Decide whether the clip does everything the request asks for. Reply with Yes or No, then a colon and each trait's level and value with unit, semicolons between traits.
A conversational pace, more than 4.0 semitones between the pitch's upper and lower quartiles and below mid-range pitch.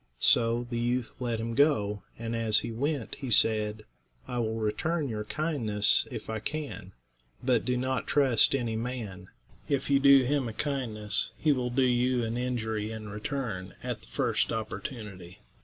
No: average, 170 wpm; average, 3.3 semitones; low, 120 Hz